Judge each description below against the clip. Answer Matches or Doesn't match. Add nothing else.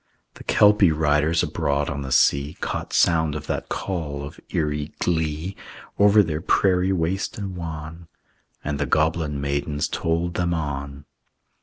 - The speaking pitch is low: Matches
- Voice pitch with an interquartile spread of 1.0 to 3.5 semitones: Matches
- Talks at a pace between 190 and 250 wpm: Doesn't match